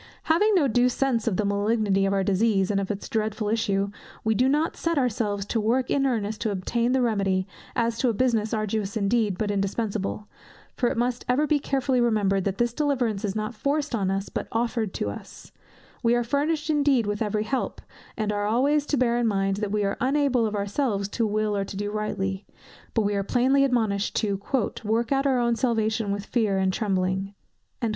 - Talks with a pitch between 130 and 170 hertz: No, high, 220 Hz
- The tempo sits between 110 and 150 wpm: No, fast, 205 wpm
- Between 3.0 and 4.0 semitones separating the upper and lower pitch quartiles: Yes, average, 3.6 semitones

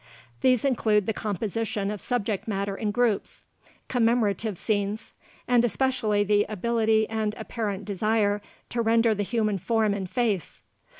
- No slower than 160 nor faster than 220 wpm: No, slow, 135 wpm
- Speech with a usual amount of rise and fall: No, narrow, 2.1 semitones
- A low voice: No, high, 215 Hz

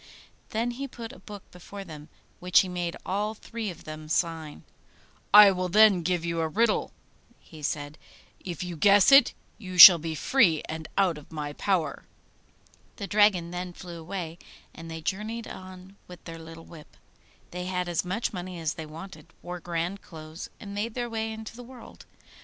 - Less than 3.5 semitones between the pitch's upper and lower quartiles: No, average, 3.9 semitones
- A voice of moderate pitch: Yes, medium, 180 Hz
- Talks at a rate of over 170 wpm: Yes, average, 180 wpm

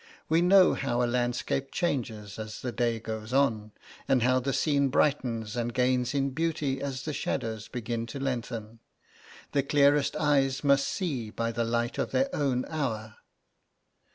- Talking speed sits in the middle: Yes, average, 160 wpm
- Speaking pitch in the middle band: No, low, 125 Hz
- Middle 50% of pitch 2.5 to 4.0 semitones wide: Yes, average, 3.3 semitones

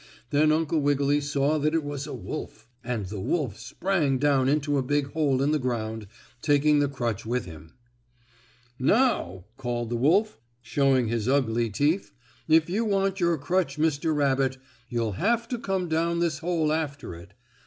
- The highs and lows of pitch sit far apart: No, average, 4.4 semitones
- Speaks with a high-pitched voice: No, medium, 145 Hz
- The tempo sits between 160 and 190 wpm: Yes, average, 170 wpm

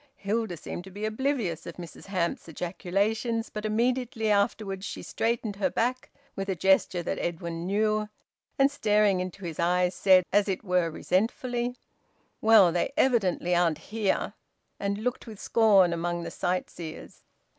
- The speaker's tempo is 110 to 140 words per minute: No, average, 150 wpm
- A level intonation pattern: No, average, 3.9 semitones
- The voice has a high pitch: Yes, high, 200 Hz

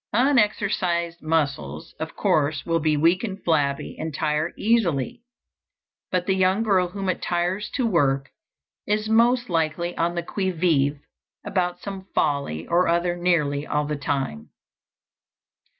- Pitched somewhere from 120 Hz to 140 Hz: No, medium, 170 Hz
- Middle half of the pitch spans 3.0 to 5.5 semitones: Yes, average, 4.3 semitones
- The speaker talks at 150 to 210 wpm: No, average, 140 wpm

